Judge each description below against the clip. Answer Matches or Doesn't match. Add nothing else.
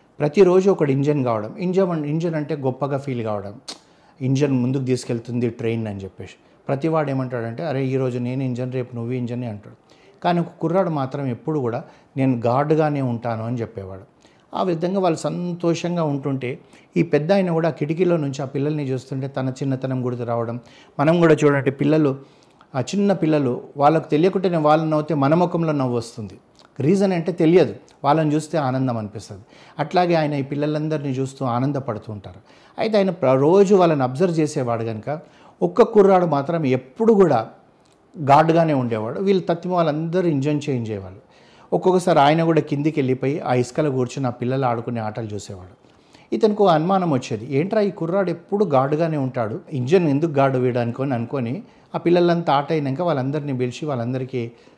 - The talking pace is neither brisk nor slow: Doesn't match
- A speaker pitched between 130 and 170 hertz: Matches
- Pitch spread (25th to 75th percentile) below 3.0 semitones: Doesn't match